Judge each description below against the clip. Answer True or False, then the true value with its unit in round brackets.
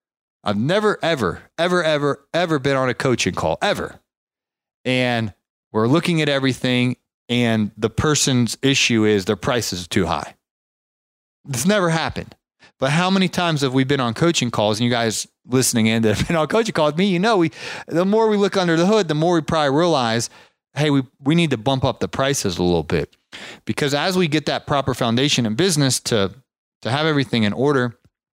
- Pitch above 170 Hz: False (135 Hz)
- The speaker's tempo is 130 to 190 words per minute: False (200 wpm)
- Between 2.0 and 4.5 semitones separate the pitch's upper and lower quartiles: False (5.3 semitones)